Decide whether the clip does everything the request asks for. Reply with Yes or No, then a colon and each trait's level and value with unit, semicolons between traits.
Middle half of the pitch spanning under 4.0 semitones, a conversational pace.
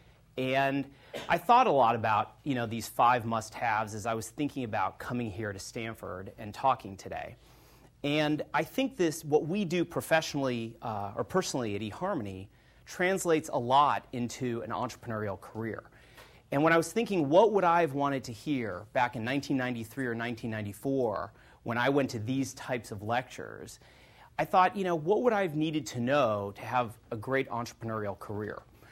No: average, 4.7 semitones; average, 175 wpm